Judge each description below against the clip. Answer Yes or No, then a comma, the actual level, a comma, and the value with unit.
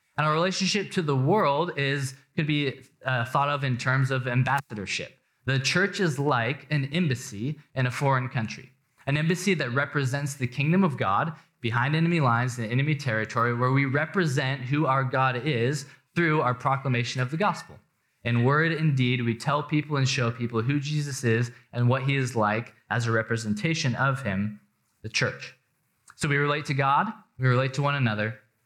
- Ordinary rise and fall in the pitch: Yes, average, 3.4 semitones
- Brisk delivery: No, average, 185 wpm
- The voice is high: No, low, 135 Hz